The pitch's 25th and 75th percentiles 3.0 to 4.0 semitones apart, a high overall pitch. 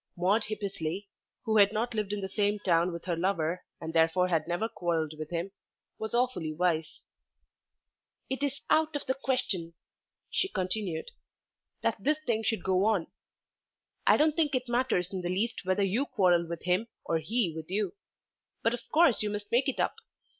No: average, 5.2 semitones; high, 195 Hz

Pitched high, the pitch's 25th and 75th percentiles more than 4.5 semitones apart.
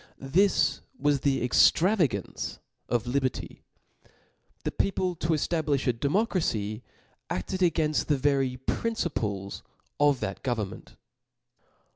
No: medium, 140 Hz; wide, 5.4 semitones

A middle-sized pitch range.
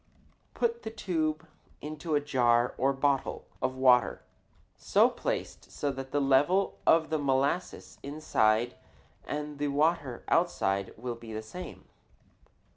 Yes: average, 3.7 semitones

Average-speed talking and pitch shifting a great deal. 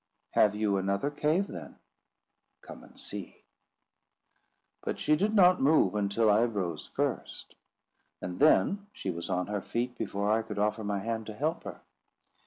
Yes: average, 160 wpm; wide, 6.6 semitones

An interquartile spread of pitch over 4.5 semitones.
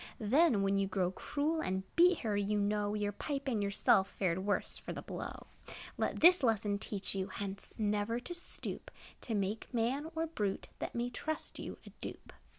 Yes: average, 5.2 semitones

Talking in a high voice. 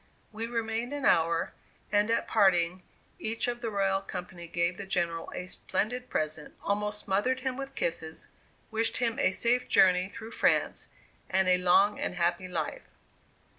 Yes: high, 195 Hz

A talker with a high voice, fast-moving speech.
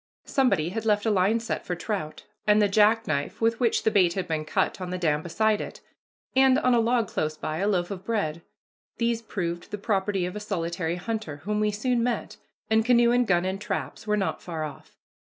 Yes: high, 205 Hz; fast, 215 wpm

